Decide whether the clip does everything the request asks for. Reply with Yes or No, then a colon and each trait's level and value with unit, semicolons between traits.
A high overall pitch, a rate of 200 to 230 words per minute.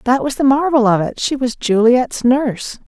Yes: very high, 250 Hz; fast, 205 wpm